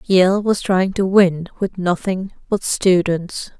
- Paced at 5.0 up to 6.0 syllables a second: No, 3.5 syllables/s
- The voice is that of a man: No, female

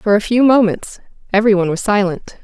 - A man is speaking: No, female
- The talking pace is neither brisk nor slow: Yes, average, 195 wpm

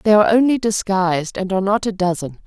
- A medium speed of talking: No, fast, 220 wpm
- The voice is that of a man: No, female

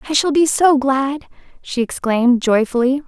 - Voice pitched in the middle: No, very high, 270 Hz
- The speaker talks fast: No, average, 155 wpm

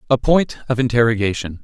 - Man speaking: Yes, male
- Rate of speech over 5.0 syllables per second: Yes, 6.0 syllables/s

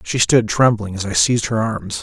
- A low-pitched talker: Yes, low, 110 Hz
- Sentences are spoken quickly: Yes, fast, 235 wpm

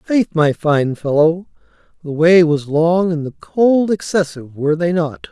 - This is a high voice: No, medium, 165 Hz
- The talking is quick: No, average, 170 wpm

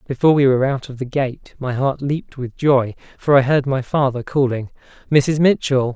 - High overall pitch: No, low, 135 Hz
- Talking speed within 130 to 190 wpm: No, average, 200 wpm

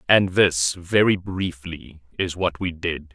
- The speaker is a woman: No, male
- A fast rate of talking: No, average, 155 wpm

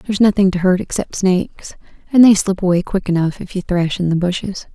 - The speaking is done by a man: No, female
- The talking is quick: Yes, fast, 215 wpm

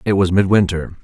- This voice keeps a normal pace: Yes, average, 175 wpm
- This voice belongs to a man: Yes, male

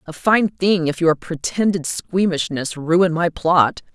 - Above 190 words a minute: No, average, 150 wpm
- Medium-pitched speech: Yes, medium, 170 Hz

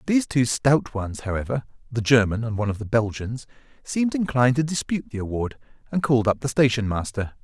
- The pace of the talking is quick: No, average, 180 wpm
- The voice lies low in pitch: Yes, low, 120 Hz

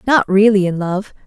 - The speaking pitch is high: Yes, high, 200 Hz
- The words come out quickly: No, average, 190 wpm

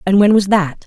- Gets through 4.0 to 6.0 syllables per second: Yes, 5.3 syllables/s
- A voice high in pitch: Yes, high, 195 Hz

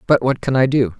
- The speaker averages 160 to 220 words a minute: No, fast, 300 wpm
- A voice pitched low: Yes, low, 125 Hz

